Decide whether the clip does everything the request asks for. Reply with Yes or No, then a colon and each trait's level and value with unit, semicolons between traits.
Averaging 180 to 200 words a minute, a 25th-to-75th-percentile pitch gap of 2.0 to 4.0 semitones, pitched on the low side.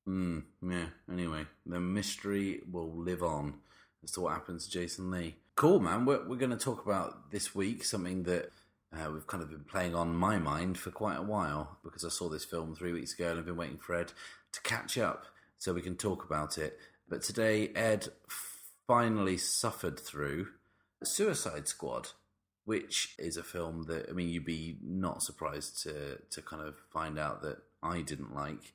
Yes: average, 195 wpm; average, 2.8 semitones; very low, 90 Hz